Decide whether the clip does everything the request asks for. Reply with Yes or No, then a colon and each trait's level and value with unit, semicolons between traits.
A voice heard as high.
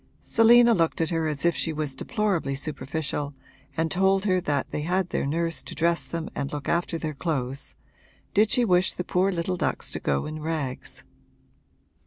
No: medium, 165 Hz